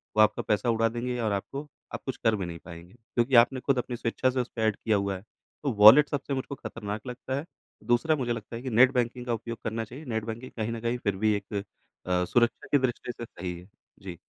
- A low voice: Yes, low, 115 Hz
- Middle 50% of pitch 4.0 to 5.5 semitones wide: No, average, 2.9 semitones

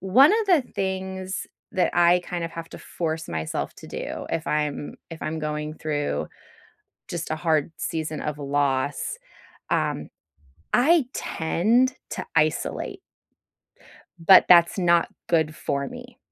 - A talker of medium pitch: Yes, medium, 165 Hz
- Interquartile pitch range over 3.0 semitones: Yes, average, 3.7 semitones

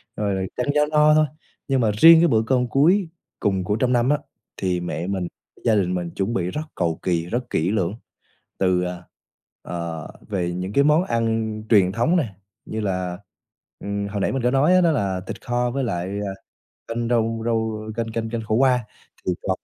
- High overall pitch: No, low, 110 Hz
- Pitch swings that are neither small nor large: Yes, average, 5.0 semitones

